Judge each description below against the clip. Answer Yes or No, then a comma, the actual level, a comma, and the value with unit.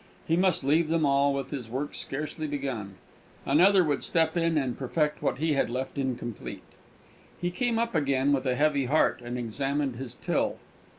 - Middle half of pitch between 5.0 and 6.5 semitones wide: No, average, 3.3 semitones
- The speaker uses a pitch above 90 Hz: Yes, medium, 140 Hz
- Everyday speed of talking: Yes, average, 180 wpm